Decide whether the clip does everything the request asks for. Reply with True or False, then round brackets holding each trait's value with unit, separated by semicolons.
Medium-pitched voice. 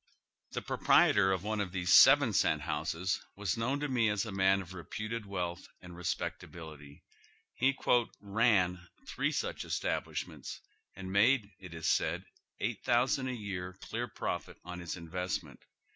False (95 Hz)